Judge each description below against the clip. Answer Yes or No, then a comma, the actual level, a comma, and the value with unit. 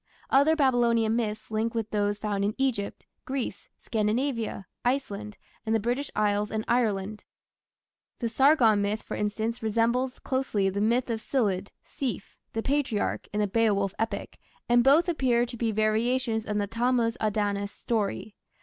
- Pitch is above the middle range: Yes, high, 225 Hz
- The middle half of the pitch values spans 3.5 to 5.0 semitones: No, average, 2.8 semitones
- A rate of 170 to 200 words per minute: No, average, 150 wpm